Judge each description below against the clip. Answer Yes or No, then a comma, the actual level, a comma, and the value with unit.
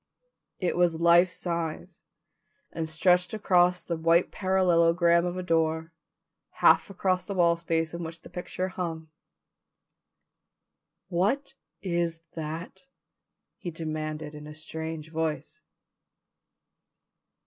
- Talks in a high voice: No, medium, 170 Hz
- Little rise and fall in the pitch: Yes, narrow, 2.0 semitones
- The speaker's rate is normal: No, slow, 110 wpm